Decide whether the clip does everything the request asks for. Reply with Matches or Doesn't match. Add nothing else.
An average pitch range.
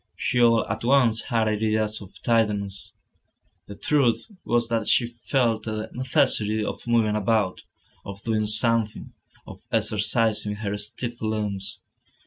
Doesn't match